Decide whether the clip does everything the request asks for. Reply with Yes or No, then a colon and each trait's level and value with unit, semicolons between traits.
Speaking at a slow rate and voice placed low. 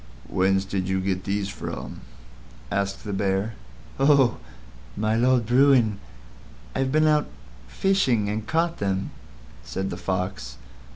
Yes: slow, 125 wpm; low, 105 Hz